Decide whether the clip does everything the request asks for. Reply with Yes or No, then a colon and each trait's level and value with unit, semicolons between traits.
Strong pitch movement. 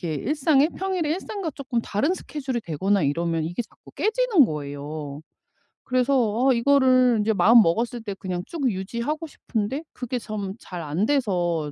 Yes: wide, 7.9 semitones